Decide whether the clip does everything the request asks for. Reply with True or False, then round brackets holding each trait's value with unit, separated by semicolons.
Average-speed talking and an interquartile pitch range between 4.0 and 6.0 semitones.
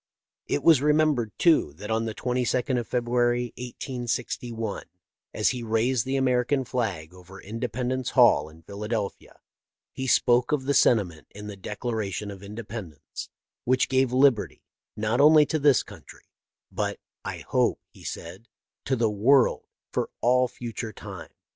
False (150 wpm; 3.5 semitones)